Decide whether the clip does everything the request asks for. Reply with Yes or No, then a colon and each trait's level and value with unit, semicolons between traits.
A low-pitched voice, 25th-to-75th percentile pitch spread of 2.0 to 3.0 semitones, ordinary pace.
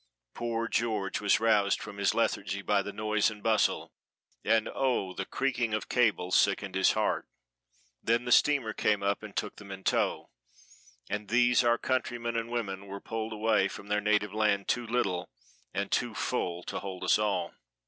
Yes: low, 105 Hz; narrow, 2.6 semitones; average, 180 wpm